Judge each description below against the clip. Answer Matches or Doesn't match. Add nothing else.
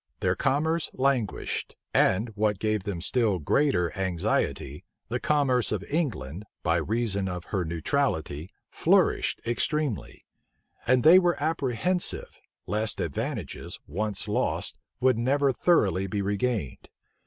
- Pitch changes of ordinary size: Doesn't match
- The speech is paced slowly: Matches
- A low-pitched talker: Matches